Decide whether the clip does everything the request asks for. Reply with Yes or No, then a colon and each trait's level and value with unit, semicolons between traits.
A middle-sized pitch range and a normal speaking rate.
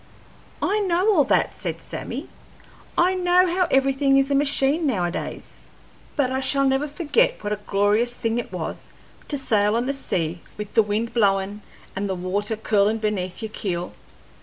No: wide, 5.8 semitones; average, 170 wpm